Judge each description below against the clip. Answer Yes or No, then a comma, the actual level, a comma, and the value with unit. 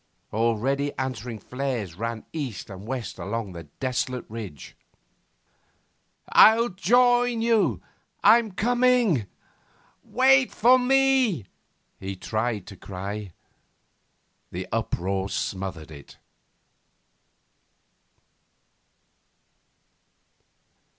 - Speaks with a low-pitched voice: Yes, low, 125 Hz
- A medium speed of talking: No, slow, 75 wpm